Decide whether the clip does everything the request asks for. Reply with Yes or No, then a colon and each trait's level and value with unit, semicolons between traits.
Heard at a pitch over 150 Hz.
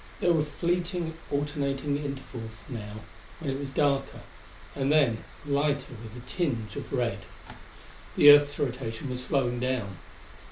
No: low, 135 Hz